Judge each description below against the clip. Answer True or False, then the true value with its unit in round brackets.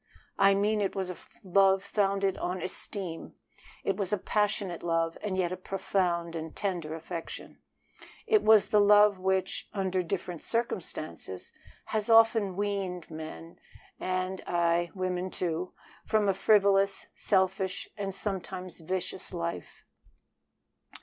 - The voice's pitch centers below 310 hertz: True (190 Hz)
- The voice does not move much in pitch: True (2.2 semitones)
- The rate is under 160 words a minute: True (135 wpm)